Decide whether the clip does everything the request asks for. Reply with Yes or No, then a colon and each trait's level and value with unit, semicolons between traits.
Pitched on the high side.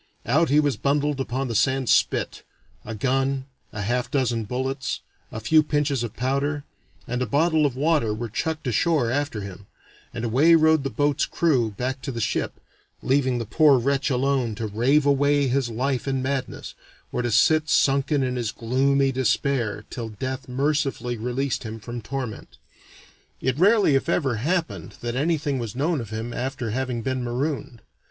No: low, 130 Hz